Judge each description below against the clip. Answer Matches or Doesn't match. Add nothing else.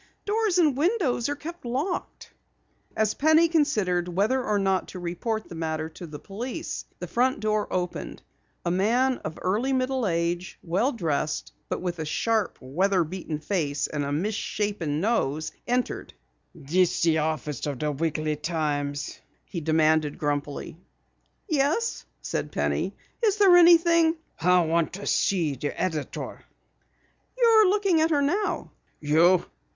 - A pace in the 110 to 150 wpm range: Matches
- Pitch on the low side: Doesn't match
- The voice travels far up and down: Matches